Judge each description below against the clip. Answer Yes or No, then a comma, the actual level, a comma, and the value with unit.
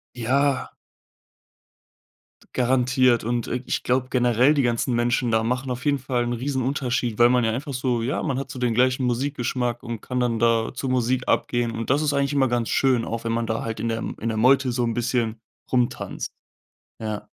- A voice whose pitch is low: Yes, low, 125 Hz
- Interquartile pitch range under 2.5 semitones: Yes, narrow, 1.9 semitones